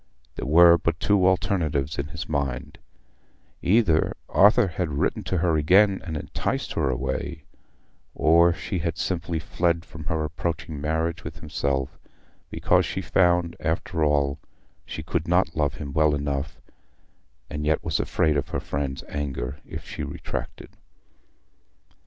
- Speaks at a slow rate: No, average, 145 wpm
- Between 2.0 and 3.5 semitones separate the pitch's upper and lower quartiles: Yes, average, 3.0 semitones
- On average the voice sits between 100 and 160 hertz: No, very low, 80 Hz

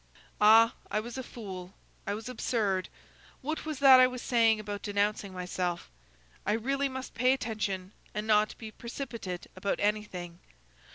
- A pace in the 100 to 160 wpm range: Yes, average, 155 wpm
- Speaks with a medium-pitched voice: No, high, 215 Hz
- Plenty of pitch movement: No, average, 3.8 semitones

